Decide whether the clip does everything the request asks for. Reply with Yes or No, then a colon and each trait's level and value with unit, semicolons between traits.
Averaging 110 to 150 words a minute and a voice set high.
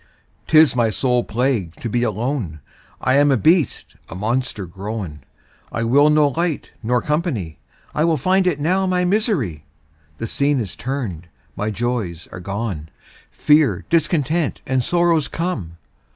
No: average, 145 wpm; low, 130 Hz